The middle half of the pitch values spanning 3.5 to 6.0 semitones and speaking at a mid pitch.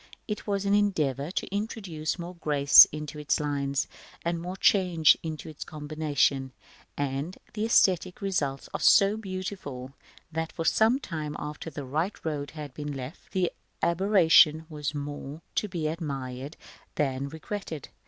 Yes: average, 4.4 semitones; medium, 155 Hz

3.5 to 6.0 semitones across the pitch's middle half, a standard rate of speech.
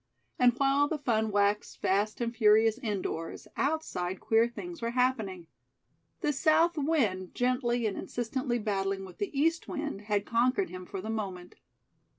Yes: average, 5.3 semitones; average, 155 wpm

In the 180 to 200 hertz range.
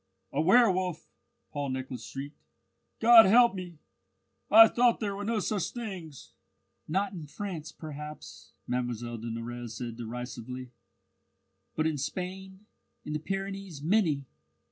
No: medium, 160 Hz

